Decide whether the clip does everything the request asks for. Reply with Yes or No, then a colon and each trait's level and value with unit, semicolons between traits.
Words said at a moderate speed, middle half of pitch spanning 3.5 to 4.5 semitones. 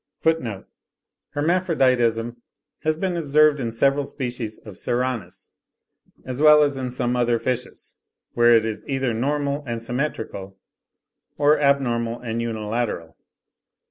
No: slow, 120 wpm; average, 3.8 semitones